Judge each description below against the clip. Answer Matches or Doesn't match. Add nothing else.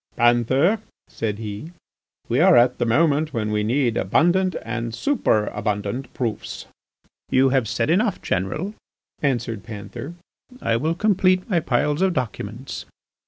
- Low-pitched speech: Matches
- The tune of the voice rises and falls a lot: Matches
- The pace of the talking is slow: Matches